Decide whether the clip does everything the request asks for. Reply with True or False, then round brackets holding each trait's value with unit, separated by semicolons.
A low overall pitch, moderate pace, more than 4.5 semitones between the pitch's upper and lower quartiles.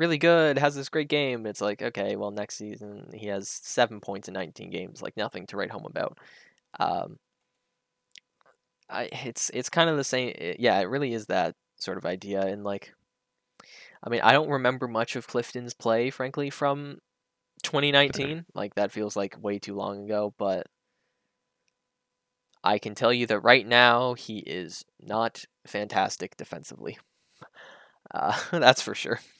True (120 Hz; 165 wpm; 5.2 semitones)